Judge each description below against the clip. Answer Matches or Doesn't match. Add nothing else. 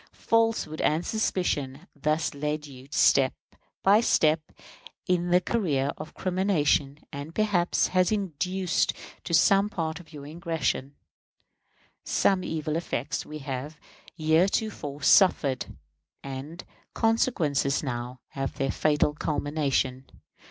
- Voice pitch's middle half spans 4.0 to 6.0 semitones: Matches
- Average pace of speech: Doesn't match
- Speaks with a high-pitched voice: Doesn't match